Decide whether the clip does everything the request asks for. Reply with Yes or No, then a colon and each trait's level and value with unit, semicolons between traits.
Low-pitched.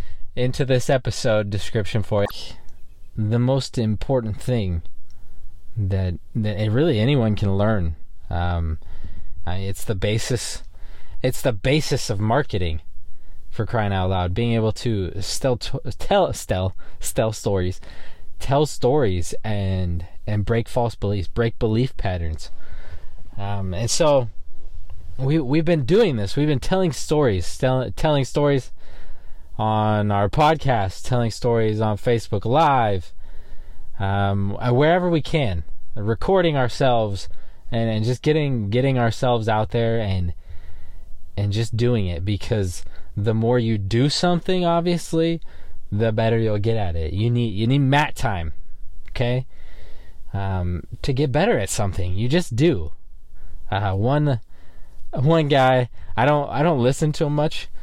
Yes: low, 105 Hz